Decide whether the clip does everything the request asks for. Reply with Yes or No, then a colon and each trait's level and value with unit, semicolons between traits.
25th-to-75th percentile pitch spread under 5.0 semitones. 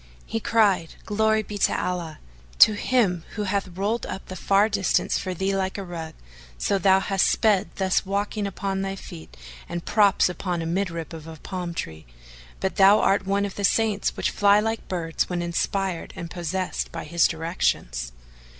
Yes: average, 2.8 semitones